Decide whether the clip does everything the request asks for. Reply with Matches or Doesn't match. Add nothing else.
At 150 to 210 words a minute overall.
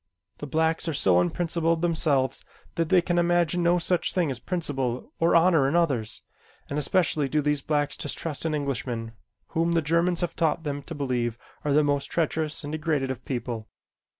Matches